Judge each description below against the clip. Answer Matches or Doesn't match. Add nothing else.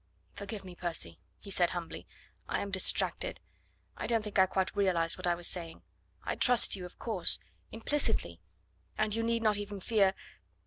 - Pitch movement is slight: Doesn't match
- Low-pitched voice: Doesn't match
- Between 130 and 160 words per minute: Doesn't match